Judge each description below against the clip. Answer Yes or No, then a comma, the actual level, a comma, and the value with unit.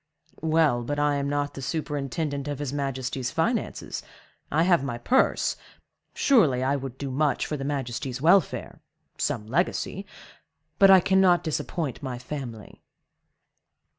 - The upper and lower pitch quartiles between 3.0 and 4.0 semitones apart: Yes, average, 3.4 semitones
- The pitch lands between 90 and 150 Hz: Yes, medium, 140 Hz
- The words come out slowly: Yes, slow, 120 wpm